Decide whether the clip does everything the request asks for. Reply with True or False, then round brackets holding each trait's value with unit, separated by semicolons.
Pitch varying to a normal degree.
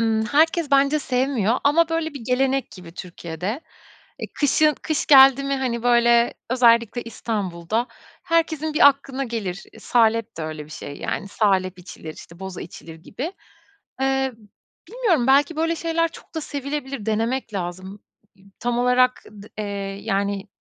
False (5.9 semitones)